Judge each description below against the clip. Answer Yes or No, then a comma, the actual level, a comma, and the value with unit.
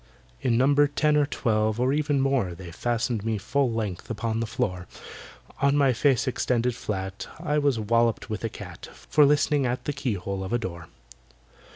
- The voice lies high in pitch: No, low, 120 Hz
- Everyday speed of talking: Yes, average, 180 wpm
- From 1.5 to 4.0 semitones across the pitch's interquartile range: No, average, 4.5 semitones